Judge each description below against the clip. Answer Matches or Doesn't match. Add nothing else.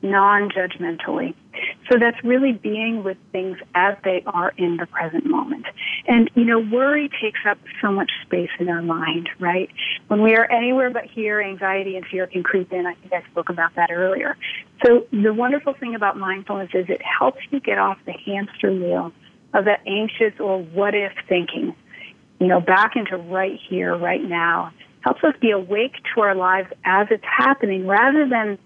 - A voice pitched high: Matches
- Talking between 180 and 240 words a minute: Matches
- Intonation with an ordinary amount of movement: Matches